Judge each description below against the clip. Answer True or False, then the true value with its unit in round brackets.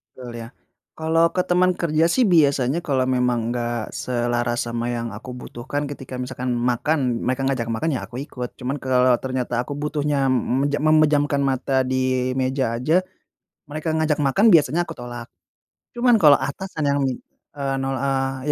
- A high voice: False (135 Hz)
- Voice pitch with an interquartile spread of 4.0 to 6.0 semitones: False (3.2 semitones)